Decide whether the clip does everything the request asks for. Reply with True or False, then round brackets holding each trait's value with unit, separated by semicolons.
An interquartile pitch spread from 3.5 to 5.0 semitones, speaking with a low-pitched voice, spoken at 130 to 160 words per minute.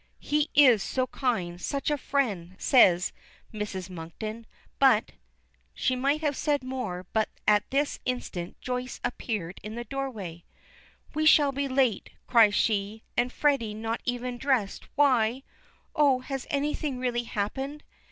False (4.6 semitones; 245 Hz; 140 wpm)